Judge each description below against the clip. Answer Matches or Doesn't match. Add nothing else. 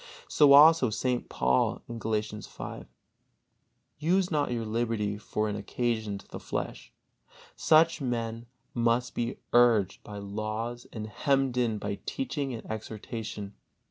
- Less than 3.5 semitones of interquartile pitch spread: Matches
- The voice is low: Matches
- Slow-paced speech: Matches